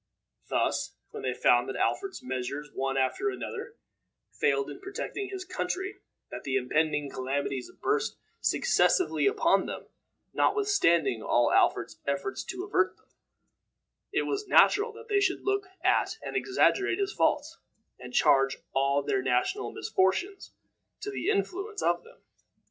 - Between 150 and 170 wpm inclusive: No, average, 140 wpm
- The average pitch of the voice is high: Yes, very high, 365 Hz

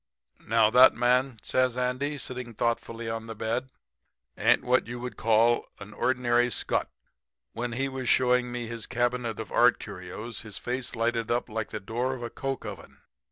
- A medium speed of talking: Yes, average, 175 wpm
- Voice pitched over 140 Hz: No, low, 120 Hz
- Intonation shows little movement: Yes, narrow, 1.8 semitones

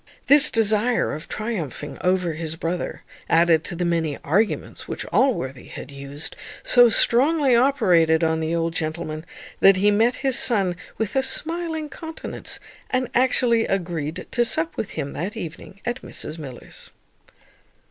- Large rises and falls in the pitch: Yes, wide, 7.3 semitones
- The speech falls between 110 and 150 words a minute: Yes, average, 145 wpm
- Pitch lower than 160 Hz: No, high, 190 Hz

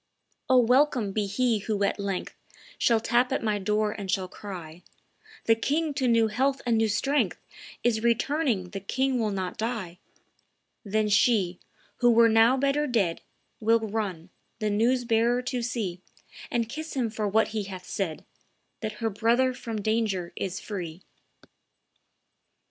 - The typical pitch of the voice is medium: No, high, 220 Hz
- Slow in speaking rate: No, average, 155 wpm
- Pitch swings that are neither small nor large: Yes, average, 3.4 semitones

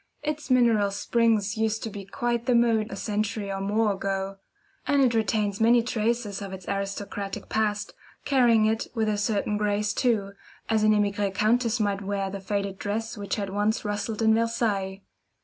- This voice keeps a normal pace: Yes, average, 175 wpm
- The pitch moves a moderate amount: No, narrow, 2.2 semitones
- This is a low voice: No, high, 210 Hz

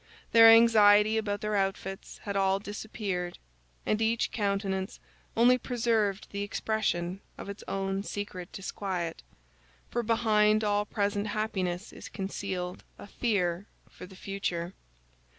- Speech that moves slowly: Yes, slow, 120 wpm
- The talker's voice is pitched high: Yes, high, 200 Hz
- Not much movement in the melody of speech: Yes, narrow, 2.1 semitones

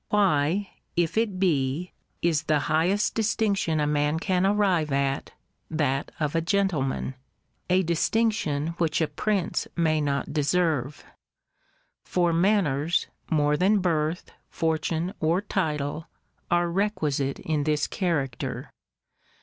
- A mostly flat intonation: No, average, 3.9 semitones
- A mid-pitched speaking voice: Yes, medium, 160 Hz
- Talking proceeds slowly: Yes, slow, 115 wpm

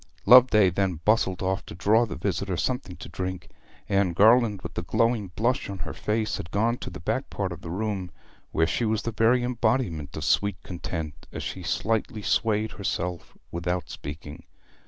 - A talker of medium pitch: No, low, 100 Hz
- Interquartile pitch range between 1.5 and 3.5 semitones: No, average, 4.3 semitones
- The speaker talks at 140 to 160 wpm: No, average, 180 wpm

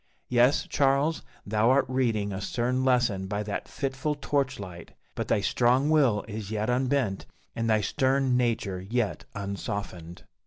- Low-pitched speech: Yes, low, 120 Hz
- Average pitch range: Yes, average, 4.4 semitones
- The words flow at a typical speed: Yes, average, 150 wpm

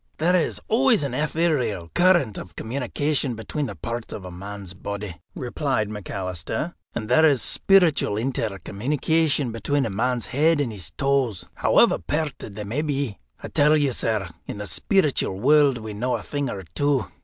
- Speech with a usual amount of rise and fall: No, wide, 6.2 semitones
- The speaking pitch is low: Yes, low, 125 Hz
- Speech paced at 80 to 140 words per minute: No, average, 165 wpm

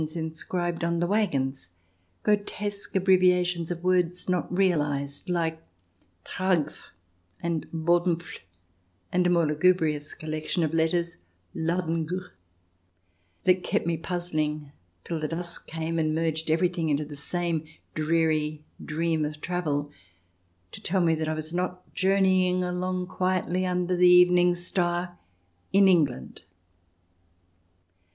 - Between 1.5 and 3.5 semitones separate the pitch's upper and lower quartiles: Yes, narrow, 2.5 semitones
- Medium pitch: Yes, medium, 170 Hz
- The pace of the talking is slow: Yes, slow, 130 wpm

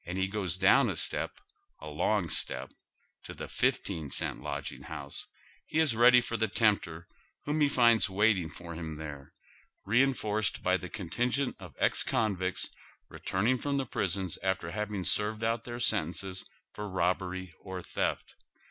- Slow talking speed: No, average, 155 wpm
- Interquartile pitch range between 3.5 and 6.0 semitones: Yes, average, 4.4 semitones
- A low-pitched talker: Yes, very low, 95 Hz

